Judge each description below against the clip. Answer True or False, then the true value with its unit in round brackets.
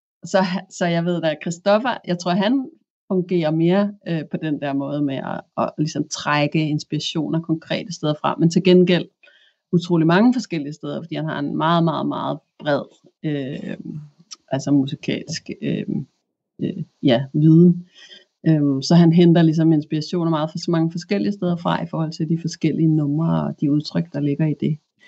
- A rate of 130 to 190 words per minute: True (180 wpm)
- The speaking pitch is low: False (165 Hz)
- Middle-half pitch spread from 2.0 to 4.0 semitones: True (2.8 semitones)